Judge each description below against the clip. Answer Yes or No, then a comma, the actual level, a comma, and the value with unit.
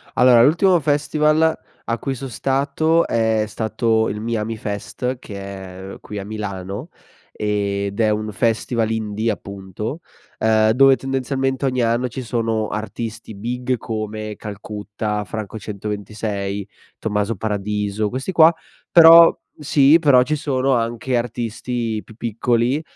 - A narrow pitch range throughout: No, average, 3.7 semitones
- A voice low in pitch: Yes, low, 115 Hz